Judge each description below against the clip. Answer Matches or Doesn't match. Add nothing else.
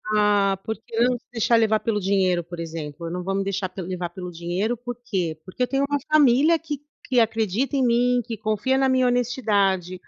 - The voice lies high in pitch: Matches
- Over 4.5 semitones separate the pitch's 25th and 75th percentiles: Matches